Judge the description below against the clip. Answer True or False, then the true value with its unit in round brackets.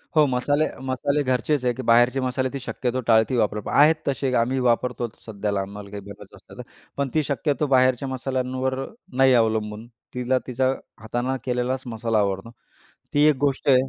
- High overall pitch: False (125 Hz)